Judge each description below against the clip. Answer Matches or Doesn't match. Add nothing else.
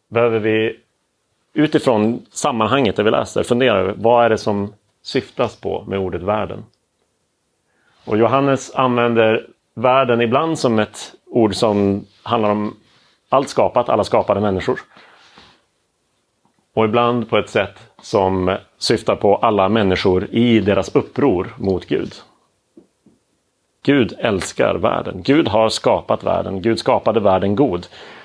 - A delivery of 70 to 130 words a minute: Matches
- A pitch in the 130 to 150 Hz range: Doesn't match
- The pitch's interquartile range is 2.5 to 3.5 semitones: Matches